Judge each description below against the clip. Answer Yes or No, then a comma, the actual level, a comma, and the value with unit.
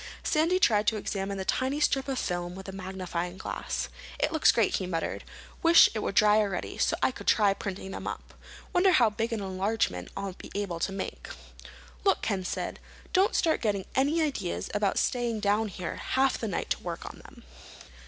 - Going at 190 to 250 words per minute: Yes, average, 195 wpm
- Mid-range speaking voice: No, high, 210 Hz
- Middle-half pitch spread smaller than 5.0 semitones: No, wide, 5.4 semitones